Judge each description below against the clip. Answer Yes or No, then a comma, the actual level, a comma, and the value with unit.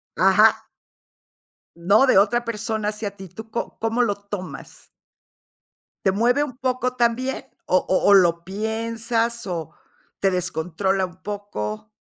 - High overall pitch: Yes, high, 210 Hz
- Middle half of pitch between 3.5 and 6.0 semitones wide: Yes, average, 3.9 semitones